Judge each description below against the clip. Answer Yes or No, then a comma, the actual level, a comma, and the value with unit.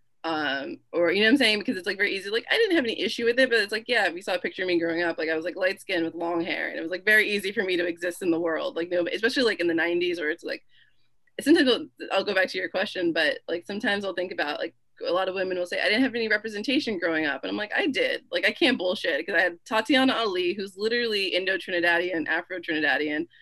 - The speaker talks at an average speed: No, fast, 280 wpm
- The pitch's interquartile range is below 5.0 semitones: No, average, 5.3 semitones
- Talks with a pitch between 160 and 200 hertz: Yes, high, 190 Hz